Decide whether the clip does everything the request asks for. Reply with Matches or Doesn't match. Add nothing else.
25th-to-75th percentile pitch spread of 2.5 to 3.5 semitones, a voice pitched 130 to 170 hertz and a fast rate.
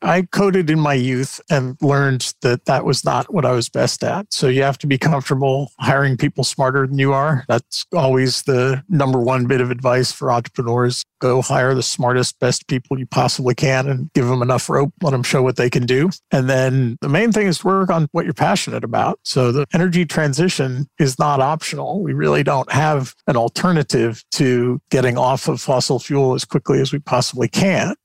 Matches